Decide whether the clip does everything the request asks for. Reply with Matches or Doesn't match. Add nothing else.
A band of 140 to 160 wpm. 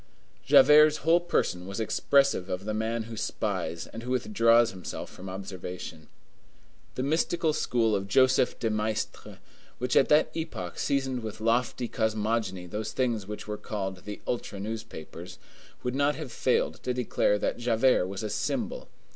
Matches